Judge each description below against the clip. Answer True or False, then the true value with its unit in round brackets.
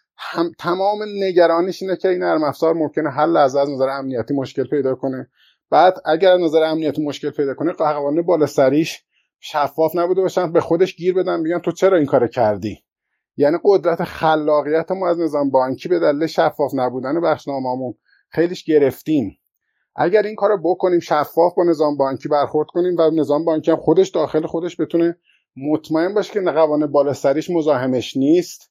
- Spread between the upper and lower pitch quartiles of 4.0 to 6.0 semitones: False (3.4 semitones)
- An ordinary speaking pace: False (170 wpm)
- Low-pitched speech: False (160 Hz)